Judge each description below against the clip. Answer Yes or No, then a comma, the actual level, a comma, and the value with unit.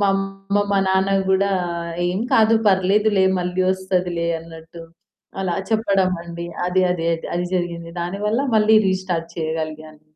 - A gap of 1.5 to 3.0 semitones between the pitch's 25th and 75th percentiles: Yes, narrow, 2.4 semitones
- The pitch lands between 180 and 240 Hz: Yes, medium, 185 Hz